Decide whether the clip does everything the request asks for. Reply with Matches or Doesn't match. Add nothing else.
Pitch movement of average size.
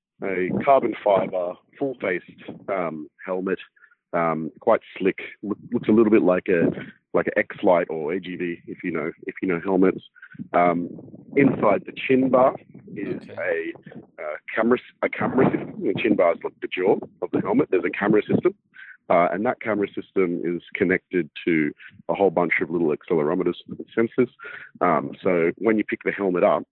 Doesn't match